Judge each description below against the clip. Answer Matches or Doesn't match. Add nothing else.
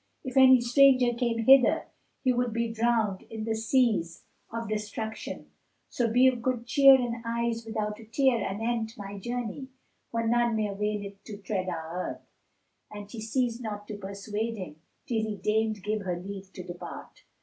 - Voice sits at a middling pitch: Doesn't match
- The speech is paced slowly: Doesn't match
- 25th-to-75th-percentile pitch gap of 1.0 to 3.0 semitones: Matches